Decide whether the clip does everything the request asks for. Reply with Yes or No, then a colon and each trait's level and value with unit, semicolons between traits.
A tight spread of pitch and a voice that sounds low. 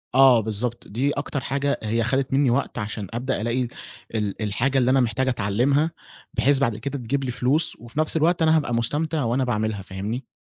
No: average, 3.6 semitones; low, 125 Hz